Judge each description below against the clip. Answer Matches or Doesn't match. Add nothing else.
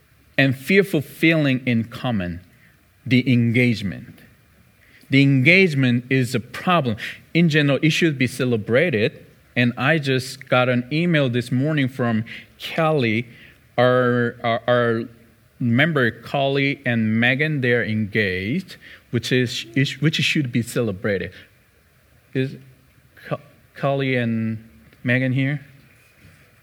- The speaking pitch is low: Matches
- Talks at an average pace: Doesn't match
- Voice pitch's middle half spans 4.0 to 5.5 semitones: Doesn't match